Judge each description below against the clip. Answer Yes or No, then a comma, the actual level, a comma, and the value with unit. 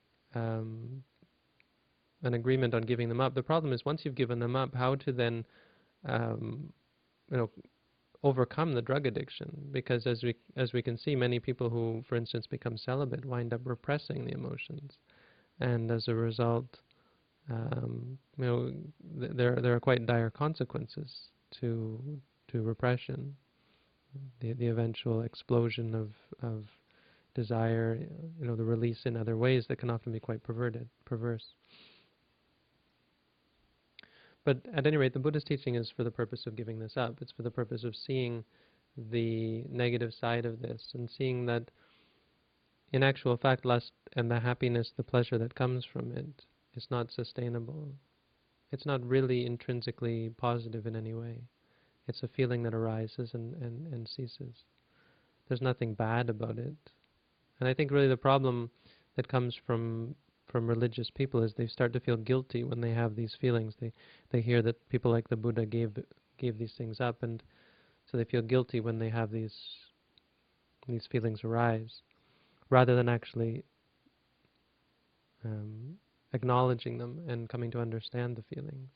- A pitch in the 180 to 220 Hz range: No, low, 120 Hz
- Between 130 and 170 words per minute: Yes, average, 160 wpm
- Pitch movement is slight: Yes, narrow, 2.1 semitones